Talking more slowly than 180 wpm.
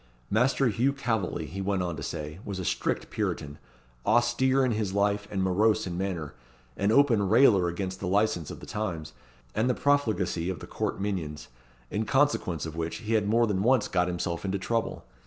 No: average, 195 wpm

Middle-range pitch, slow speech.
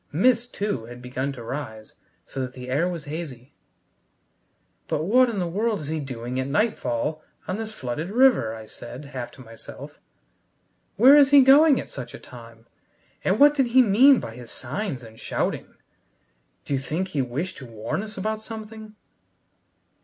No: medium, 155 Hz; average, 175 wpm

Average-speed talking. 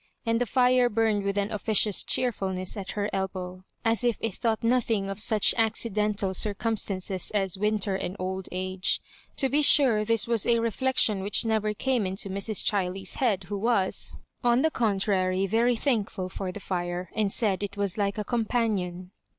Yes: average, 175 wpm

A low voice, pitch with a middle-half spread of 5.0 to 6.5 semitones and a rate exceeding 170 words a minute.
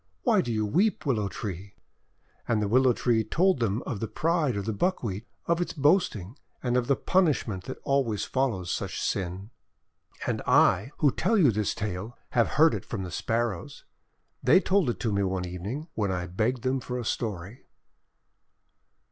Yes: low, 115 Hz; average, 5.3 semitones; average, 180 wpm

